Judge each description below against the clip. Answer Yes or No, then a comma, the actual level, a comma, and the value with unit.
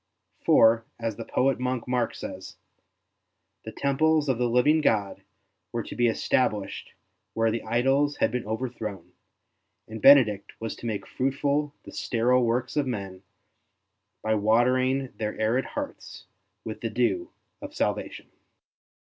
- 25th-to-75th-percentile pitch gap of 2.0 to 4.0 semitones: Yes, average, 3.4 semitones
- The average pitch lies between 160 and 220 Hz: No, low, 120 Hz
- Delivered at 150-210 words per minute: No, average, 140 wpm